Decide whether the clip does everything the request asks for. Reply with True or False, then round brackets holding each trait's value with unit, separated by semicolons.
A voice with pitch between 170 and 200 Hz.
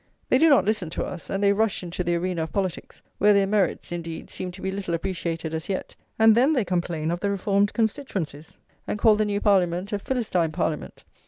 True (190 Hz)